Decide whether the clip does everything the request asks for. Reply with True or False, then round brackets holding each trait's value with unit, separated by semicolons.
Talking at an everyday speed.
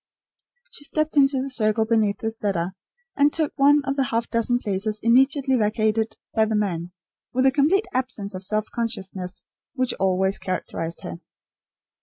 True (160 wpm)